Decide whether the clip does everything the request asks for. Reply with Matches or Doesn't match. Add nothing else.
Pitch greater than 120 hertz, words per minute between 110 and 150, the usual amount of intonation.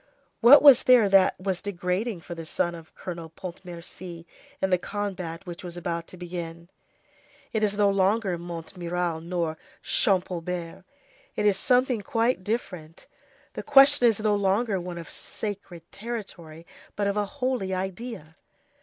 Matches